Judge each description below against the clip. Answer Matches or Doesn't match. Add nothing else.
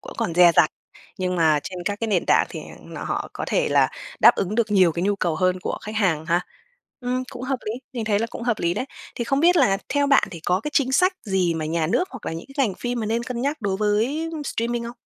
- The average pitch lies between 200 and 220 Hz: Matches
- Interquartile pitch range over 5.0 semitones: Matches